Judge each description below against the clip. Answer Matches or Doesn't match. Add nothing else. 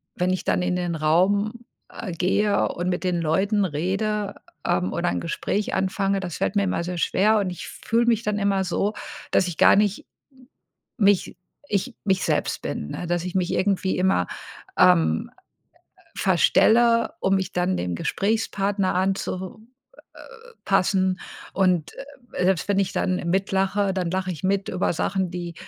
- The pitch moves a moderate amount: Doesn't match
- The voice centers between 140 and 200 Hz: Matches